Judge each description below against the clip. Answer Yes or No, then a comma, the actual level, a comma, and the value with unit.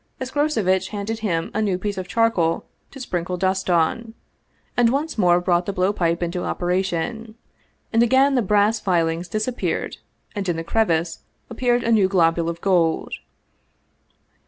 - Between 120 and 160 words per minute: Yes, average, 155 wpm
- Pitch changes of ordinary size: Yes, average, 4.5 semitones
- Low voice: No, high, 190 Hz